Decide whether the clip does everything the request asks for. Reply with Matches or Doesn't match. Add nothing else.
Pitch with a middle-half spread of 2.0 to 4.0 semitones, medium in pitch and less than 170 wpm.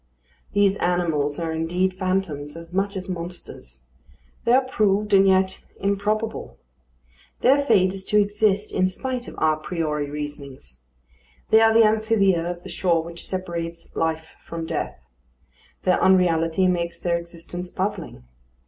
Matches